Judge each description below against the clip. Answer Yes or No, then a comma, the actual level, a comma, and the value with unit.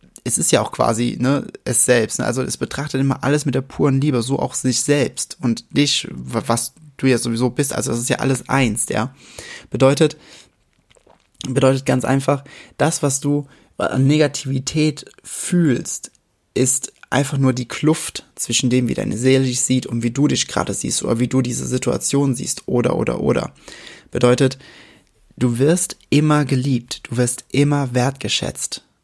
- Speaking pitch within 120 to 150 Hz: Yes, low, 135 Hz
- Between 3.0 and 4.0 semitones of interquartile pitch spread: No, narrow, 2.6 semitones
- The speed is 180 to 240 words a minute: No, average, 170 wpm